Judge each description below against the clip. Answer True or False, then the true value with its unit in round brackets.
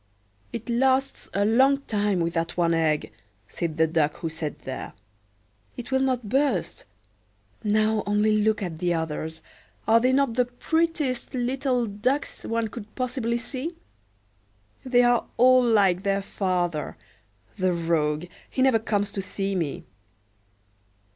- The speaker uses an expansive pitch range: True (6.3 semitones)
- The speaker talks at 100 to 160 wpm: True (140 wpm)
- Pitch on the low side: False (215 Hz)